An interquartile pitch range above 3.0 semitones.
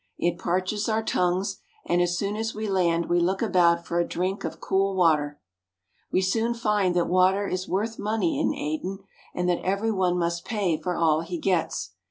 No: narrow, 2.6 semitones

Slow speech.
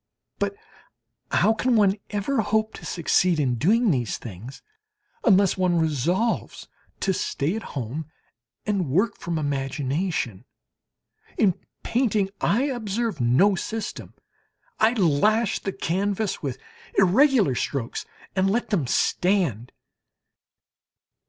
Yes: slow, 115 wpm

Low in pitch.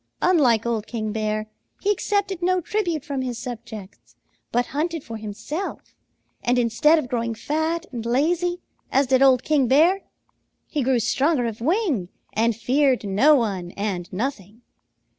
No: very high, 255 Hz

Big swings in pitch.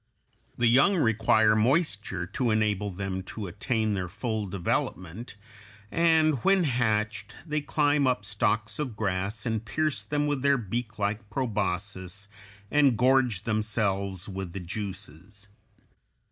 No: average, 4.3 semitones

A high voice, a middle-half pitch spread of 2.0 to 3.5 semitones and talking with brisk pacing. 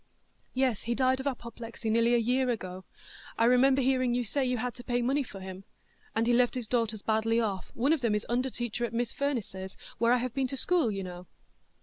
Yes: high, 240 Hz; narrow, 2.6 semitones; fast, 225 wpm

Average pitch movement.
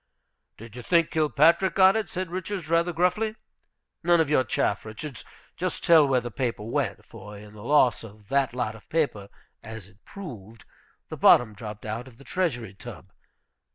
No: wide, 7.5 semitones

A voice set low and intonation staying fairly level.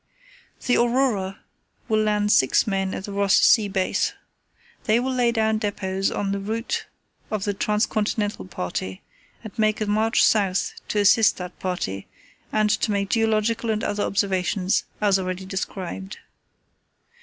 No: high, 205 Hz; narrow, 2.2 semitones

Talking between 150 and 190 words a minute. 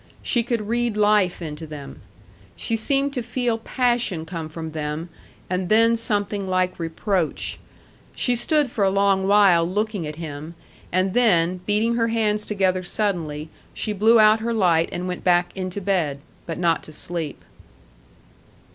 Yes: average, 155 wpm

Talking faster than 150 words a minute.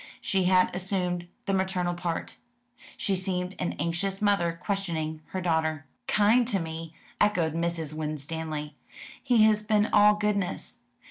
No: slow, 135 wpm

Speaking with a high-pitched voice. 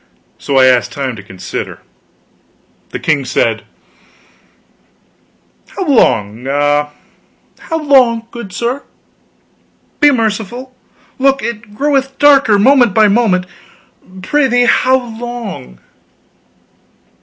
Yes: high, 230 Hz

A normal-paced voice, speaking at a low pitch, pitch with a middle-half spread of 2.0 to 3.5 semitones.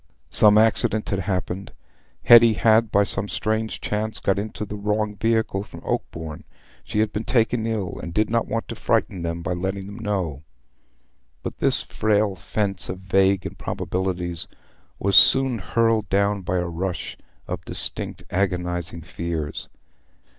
Yes: average, 150 wpm; low, 100 Hz; average, 3.2 semitones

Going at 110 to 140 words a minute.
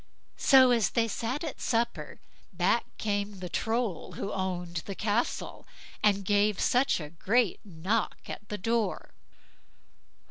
Yes: slow, 135 wpm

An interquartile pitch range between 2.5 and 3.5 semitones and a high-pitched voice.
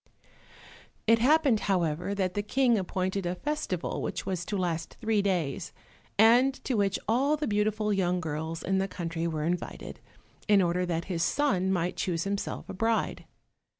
No: average, 3.9 semitones; high, 195 Hz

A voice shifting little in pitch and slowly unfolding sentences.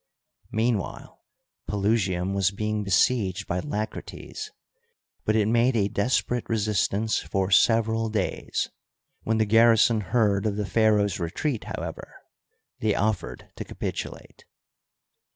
Yes: narrow, 2.2 semitones; slow, 115 wpm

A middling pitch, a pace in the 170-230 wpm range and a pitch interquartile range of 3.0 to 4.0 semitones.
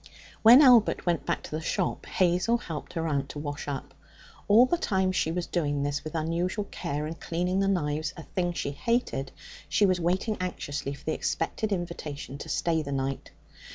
No: medium, 170 Hz; average, 190 wpm; average, 4.4 semitones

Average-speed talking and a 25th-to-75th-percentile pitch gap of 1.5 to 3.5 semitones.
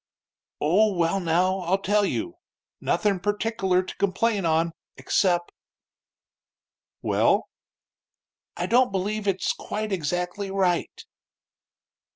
No: slow, 105 wpm; narrow, 2.6 semitones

